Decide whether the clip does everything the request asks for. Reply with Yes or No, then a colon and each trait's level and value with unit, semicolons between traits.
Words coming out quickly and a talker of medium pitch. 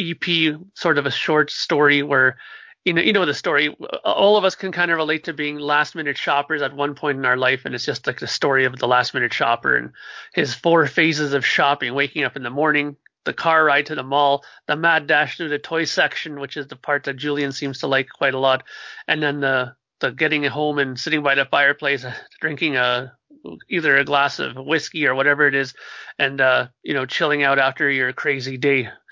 Yes: fast, 225 wpm; medium, 145 Hz